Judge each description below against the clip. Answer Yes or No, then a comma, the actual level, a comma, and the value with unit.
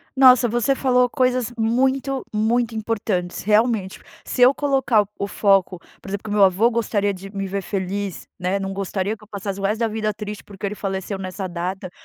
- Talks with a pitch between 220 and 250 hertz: No, high, 210 Hz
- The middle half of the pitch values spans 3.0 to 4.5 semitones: Yes, average, 3.3 semitones